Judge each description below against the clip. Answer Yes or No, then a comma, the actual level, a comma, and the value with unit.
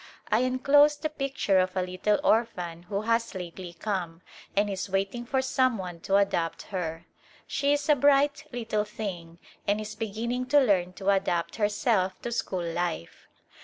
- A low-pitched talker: No, high, 205 Hz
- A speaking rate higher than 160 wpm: Yes, average, 170 wpm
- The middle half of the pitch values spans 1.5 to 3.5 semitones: No, average, 5.0 semitones